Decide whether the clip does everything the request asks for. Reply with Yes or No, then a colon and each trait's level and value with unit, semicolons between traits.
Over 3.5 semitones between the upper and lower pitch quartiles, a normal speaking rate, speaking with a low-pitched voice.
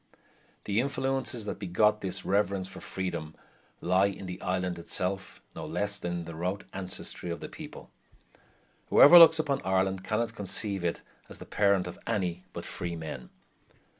No: average, 2.8 semitones; average, 160 wpm; very low, 95 Hz